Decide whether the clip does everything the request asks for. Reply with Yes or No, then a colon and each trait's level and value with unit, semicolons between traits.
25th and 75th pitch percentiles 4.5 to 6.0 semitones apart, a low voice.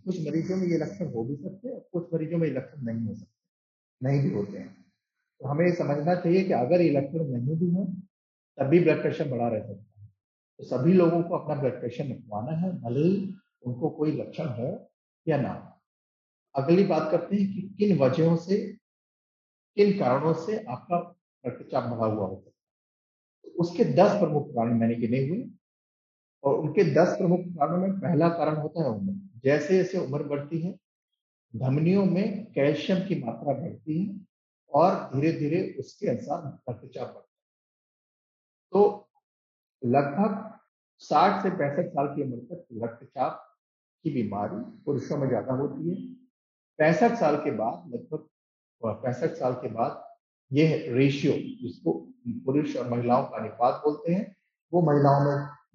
No: average, 5.1 semitones; medium, 160 Hz